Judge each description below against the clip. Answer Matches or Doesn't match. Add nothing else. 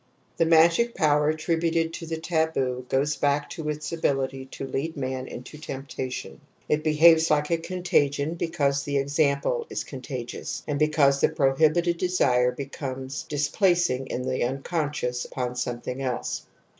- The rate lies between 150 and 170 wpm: Matches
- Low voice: Doesn't match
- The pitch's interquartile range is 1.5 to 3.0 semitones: Doesn't match